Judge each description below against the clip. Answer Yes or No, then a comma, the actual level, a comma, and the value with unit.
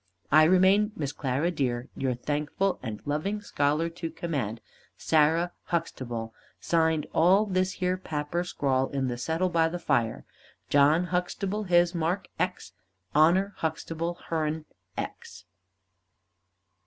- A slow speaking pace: Yes, slow, 125 wpm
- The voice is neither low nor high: Yes, medium, 160 Hz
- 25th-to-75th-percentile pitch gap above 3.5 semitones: Yes, average, 3.9 semitones